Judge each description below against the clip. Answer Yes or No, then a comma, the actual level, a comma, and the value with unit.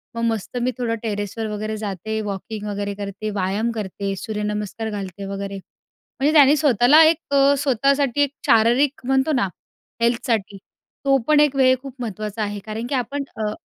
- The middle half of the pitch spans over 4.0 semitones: Yes, average, 4.4 semitones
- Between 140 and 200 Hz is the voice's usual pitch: No, high, 225 Hz